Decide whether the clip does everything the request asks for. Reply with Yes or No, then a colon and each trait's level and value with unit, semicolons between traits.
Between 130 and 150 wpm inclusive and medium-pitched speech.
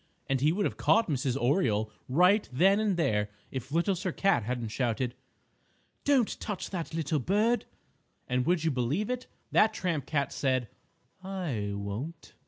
No: average, 160 wpm; medium, 155 Hz